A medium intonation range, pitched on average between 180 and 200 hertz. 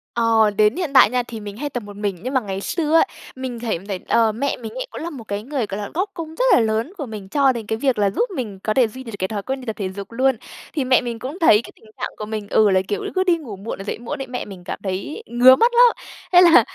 No: average, 4.7 semitones; high, 235 Hz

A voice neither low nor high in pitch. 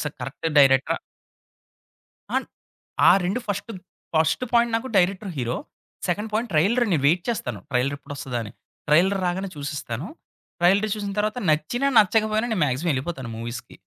Yes: medium, 175 Hz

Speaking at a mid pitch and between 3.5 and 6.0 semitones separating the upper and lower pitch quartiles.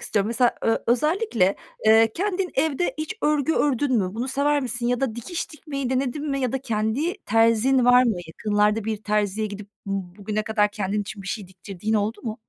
No: high, 225 Hz; average, 4.5 semitones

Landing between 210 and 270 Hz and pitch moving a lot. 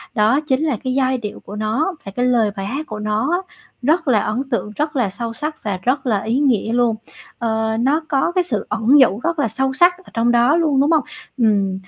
No: very high, 250 Hz; average, 5.0 semitones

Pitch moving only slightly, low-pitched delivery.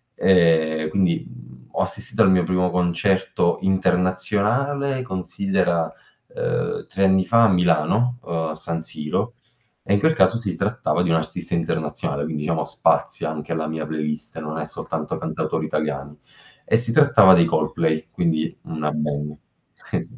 No: average, 3.9 semitones; very low, 85 Hz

